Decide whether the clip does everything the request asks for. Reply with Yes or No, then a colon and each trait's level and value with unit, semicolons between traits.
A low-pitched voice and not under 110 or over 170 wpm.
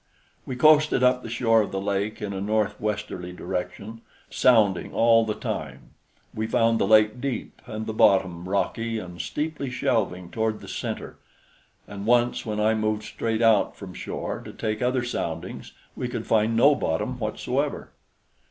Yes: low, 110 Hz; average, 165 wpm